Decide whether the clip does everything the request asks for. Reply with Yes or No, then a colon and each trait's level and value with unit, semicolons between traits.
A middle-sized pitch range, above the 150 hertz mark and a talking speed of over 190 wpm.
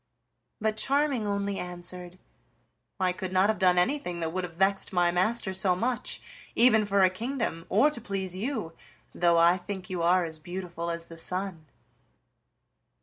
No: average, 3.2 semitones; medium, 185 Hz; average, 165 wpm